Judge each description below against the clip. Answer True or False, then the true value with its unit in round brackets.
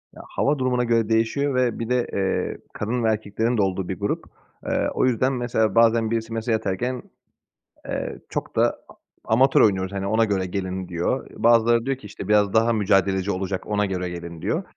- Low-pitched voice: True (110 Hz)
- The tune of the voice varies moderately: True (3.4 semitones)